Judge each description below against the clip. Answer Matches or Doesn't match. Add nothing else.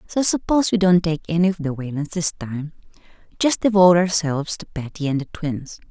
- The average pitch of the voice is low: Doesn't match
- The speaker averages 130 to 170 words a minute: Doesn't match